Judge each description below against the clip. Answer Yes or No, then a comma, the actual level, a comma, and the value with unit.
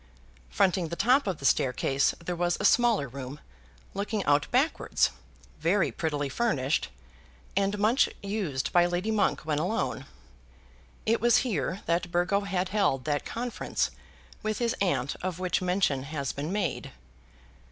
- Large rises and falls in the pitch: Yes, wide, 6.1 semitones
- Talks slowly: No, average, 145 wpm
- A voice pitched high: No, medium, 180 Hz